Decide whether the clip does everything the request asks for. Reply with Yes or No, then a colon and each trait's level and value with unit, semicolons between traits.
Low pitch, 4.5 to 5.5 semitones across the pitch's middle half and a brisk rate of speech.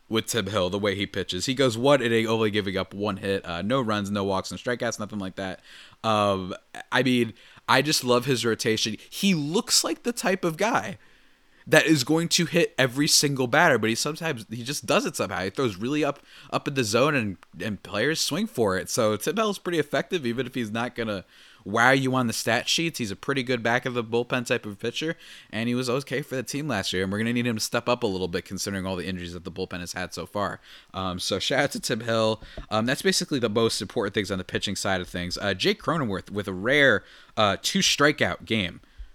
Yes: low, 115 Hz; average, 5.2 semitones; fast, 245 wpm